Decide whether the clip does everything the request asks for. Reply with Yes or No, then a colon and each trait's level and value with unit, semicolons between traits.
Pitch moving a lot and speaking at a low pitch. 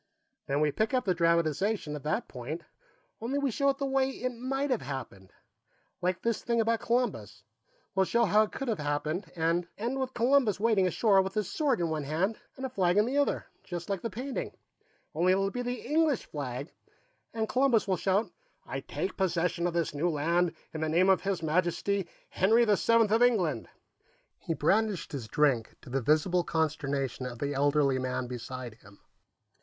No: wide, 7.2 semitones; medium, 185 Hz